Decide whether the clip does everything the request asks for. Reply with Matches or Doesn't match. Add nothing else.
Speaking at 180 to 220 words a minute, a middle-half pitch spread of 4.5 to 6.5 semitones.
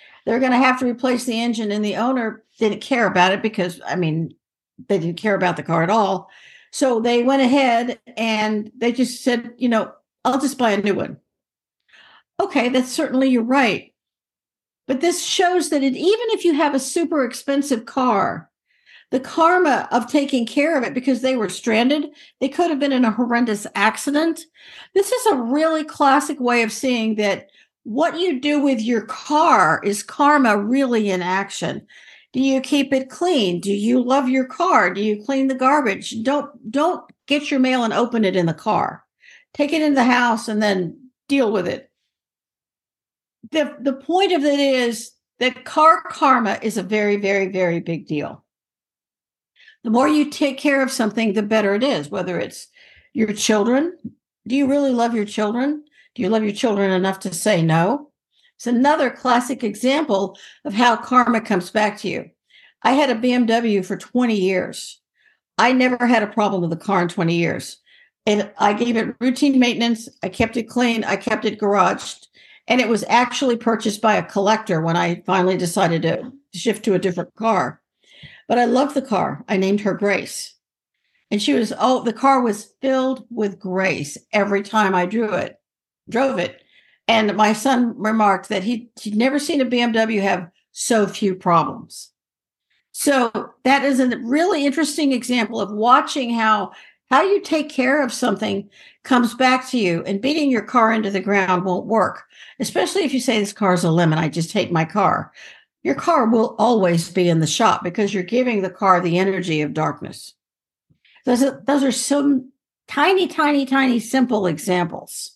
Matches